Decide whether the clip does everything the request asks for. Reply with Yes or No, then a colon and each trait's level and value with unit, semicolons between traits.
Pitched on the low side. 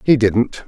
Yes: low, 115 Hz